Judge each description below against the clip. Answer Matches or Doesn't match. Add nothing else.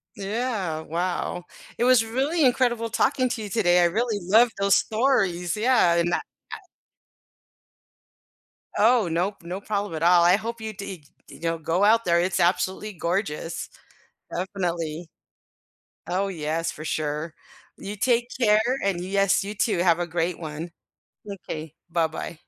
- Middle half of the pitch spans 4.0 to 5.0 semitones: Matches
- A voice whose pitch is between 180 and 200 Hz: Matches